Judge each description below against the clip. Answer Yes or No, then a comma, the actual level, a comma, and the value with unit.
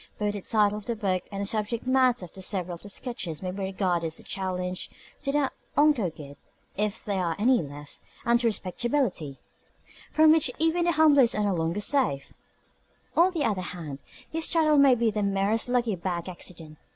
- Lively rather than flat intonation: Yes, wide, 5.8 semitones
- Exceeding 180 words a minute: Yes, average, 195 wpm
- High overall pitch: Yes, high, 205 Hz